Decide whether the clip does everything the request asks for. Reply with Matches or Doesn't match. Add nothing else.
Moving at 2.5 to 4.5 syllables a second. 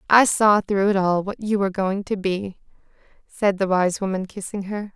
Doesn't match